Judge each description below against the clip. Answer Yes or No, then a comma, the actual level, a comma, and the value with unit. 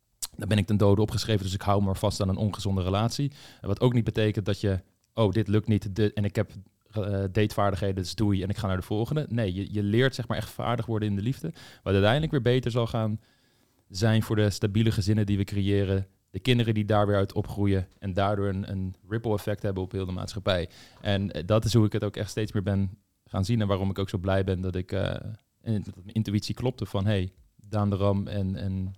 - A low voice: Yes, low, 105 Hz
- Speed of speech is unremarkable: No, fast, 245 wpm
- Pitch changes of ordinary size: No, narrow, 2.1 semitones